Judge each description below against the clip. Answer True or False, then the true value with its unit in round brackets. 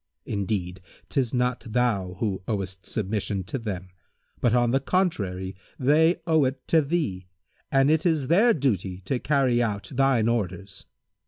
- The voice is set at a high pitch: False (120 Hz)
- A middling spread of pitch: False (6.1 semitones)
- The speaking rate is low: False (150 wpm)